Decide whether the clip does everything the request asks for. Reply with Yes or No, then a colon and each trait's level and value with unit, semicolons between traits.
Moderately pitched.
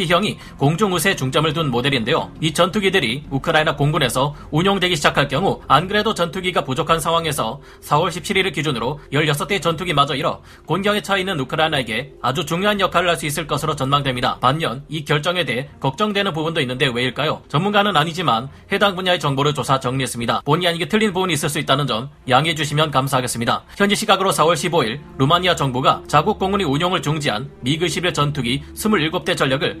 Yes: medium, 160 Hz